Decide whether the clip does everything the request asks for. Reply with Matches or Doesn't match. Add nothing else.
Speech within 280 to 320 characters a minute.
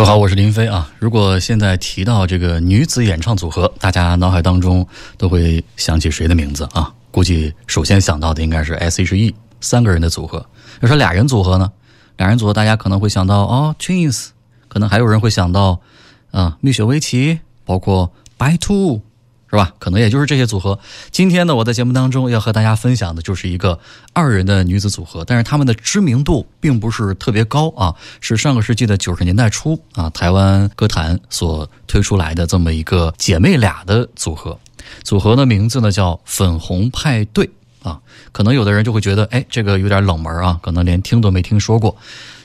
Matches